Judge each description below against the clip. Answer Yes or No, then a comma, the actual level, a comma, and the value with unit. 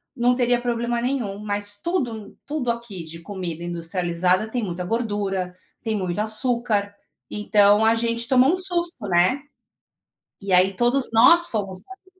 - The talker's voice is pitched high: Yes, high, 215 Hz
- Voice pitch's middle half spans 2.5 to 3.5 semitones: No, average, 4.3 semitones